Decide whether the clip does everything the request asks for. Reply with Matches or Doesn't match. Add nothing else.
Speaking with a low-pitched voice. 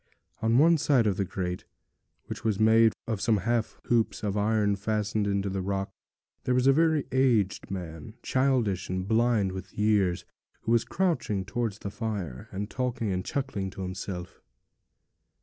Matches